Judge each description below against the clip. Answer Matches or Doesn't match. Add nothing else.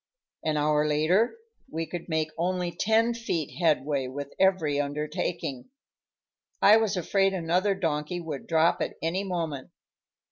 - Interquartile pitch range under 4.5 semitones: Matches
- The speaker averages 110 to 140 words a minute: Matches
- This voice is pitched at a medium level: Matches